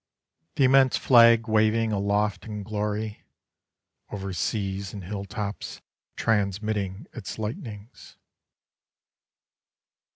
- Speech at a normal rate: No, slow, 85 wpm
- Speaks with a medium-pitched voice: No, low, 105 Hz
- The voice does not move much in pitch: Yes, narrow, 1.8 semitones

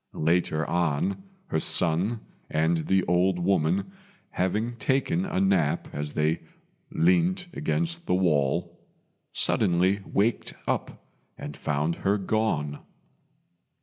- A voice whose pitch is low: Yes, very low, 90 Hz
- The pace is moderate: No, slow, 110 wpm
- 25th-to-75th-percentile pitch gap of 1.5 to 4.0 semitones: No, wide, 5.6 semitones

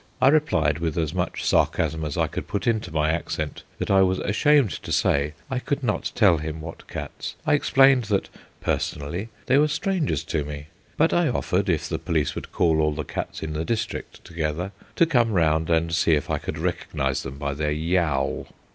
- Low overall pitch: Yes, very low, 85 Hz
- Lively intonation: Yes, wide, 7.0 semitones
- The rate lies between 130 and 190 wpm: No, average, 200 wpm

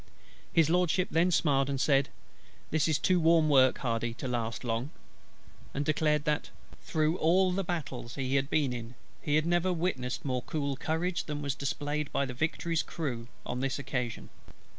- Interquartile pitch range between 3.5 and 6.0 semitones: Yes, average, 3.8 semitones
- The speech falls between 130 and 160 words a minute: No, average, 175 wpm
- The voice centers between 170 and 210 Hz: No, medium, 145 Hz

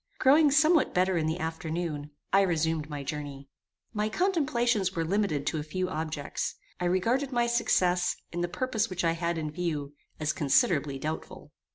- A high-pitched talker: No, medium, 175 Hz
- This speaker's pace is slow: No, average, 170 wpm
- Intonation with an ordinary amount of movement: No, wide, 5.7 semitones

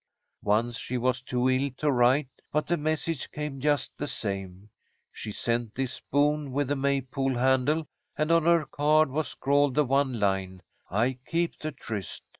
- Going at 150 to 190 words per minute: Yes, average, 175 wpm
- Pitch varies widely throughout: No, average, 3.5 semitones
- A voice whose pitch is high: No, low, 135 Hz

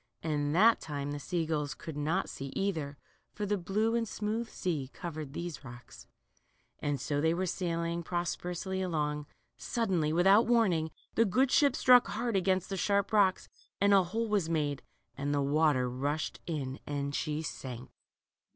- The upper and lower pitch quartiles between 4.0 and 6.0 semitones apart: Yes, average, 5.2 semitones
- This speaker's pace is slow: No, average, 170 wpm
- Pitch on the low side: No, medium, 170 Hz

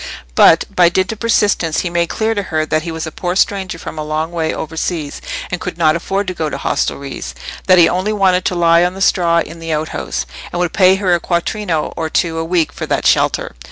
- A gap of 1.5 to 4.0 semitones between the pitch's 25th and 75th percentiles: Yes, narrow, 2.5 semitones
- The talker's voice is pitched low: No, medium, 170 Hz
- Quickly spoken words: Yes, fast, 240 wpm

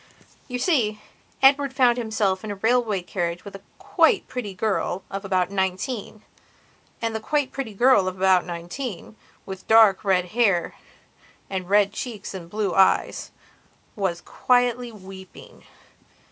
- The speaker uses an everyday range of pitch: Yes, average, 4.2 semitones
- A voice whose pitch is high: Yes, high, 205 Hz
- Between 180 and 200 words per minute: No, slow, 135 wpm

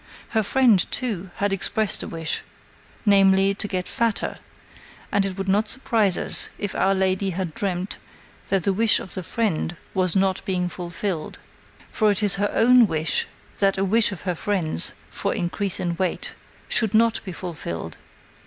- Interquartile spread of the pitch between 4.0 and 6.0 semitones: No, narrow, 2.4 semitones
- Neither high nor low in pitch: No, high, 195 Hz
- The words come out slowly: No, average, 170 wpm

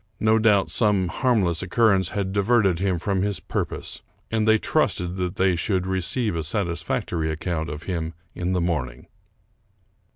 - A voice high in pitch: No, very low, 95 Hz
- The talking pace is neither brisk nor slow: Yes, average, 155 wpm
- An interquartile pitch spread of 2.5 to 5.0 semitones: Yes, average, 3.3 semitones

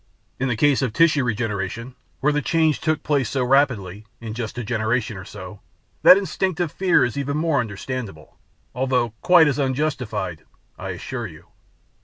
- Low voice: Yes, low, 125 Hz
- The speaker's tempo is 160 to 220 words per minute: Yes, average, 165 wpm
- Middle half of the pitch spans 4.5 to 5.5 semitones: Yes, average, 5.1 semitones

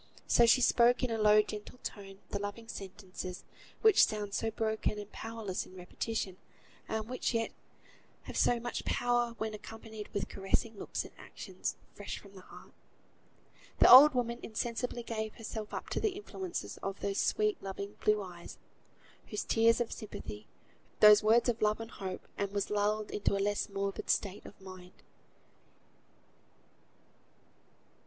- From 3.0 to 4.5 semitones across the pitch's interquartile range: No, narrow, 2.6 semitones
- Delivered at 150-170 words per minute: Yes, average, 160 wpm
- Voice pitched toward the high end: Yes, high, 215 Hz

